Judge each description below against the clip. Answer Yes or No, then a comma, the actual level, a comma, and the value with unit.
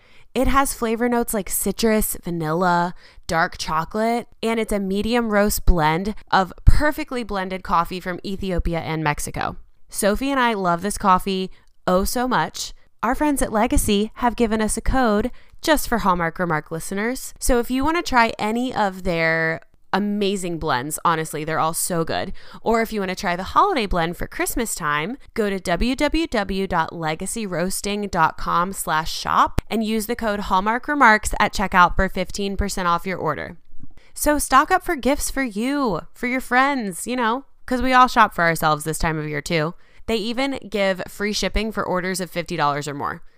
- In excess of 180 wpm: No, average, 175 wpm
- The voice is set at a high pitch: Yes, high, 200 Hz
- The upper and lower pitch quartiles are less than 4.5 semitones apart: No, wide, 5.5 semitones